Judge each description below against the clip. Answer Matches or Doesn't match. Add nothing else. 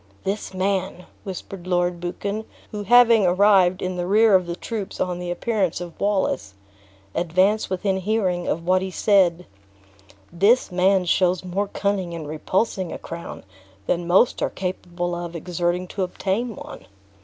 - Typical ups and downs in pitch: Doesn't match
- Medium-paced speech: Matches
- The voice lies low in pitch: Doesn't match